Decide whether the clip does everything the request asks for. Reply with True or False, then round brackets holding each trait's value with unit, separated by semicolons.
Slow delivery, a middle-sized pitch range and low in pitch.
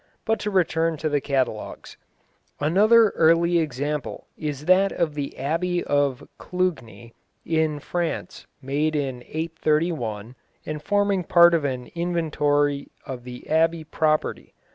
False (125 wpm; 3.3 semitones; 155 Hz)